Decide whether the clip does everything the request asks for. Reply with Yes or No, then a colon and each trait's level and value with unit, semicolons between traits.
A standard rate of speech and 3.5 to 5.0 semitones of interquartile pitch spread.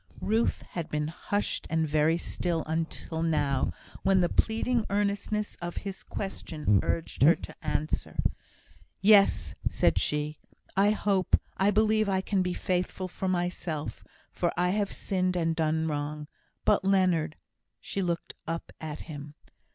Yes: average, 145 wpm; average, 3.9 semitones